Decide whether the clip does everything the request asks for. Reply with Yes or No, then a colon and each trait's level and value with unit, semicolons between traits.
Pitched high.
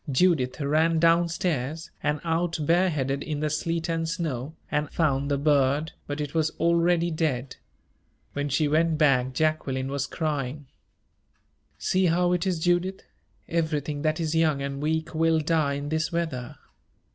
No: medium, 155 Hz